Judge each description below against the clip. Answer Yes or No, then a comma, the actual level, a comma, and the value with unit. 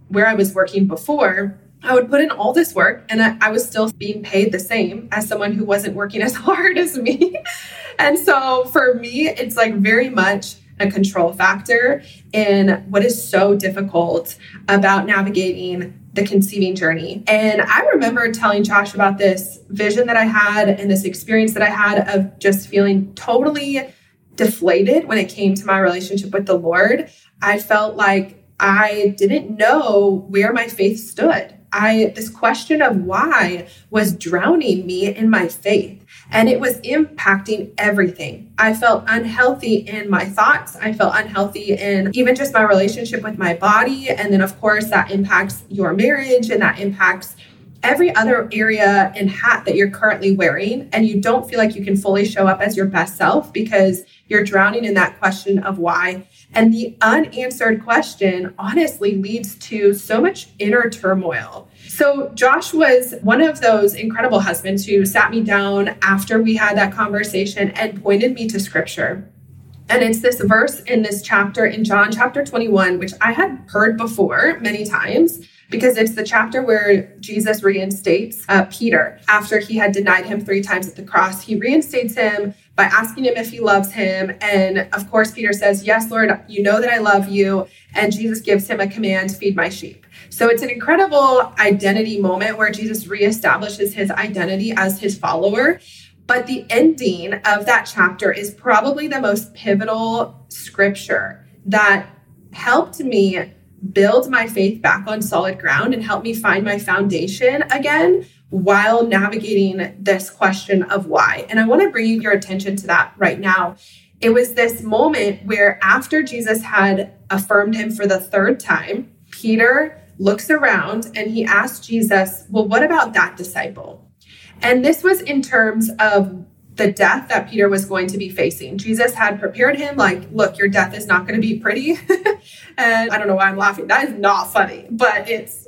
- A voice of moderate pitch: No, high, 210 Hz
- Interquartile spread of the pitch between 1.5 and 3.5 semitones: Yes, average, 2.7 semitones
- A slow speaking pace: No, average, 175 wpm